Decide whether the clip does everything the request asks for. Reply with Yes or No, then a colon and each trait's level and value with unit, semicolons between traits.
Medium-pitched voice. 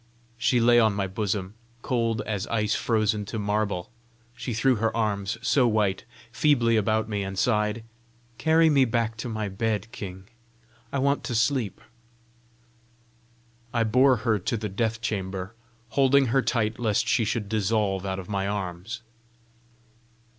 No: low, 110 Hz